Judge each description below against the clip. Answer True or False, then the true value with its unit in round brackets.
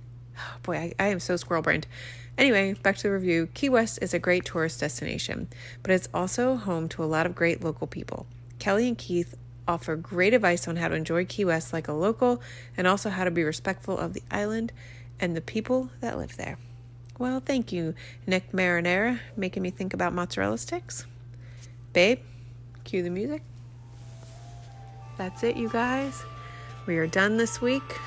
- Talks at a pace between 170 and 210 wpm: True (180 wpm)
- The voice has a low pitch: False (165 Hz)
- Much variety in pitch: True (7.7 semitones)